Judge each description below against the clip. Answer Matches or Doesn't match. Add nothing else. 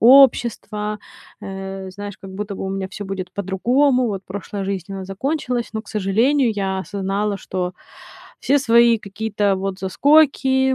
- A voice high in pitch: Matches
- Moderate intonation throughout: Matches